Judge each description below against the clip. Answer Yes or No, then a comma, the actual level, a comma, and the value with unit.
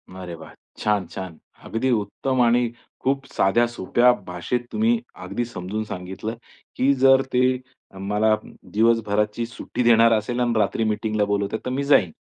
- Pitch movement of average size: Yes, average, 3.3 semitones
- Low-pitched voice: Yes, low, 110 Hz